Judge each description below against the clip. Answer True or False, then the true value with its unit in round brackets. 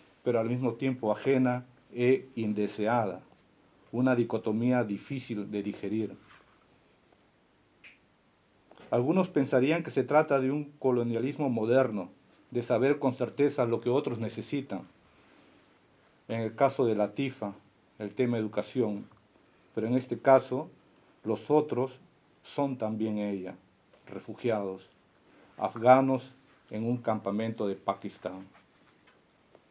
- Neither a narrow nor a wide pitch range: True (4.0 semitones)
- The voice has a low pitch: True (120 Hz)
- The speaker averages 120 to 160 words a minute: False (110 wpm)